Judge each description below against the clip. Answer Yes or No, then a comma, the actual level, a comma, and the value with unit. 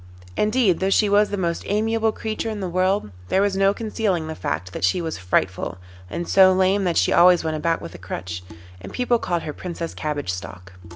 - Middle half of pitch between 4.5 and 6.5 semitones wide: Yes, average, 5.2 semitones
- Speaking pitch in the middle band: Yes, medium, 180 Hz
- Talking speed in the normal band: No, fast, 215 wpm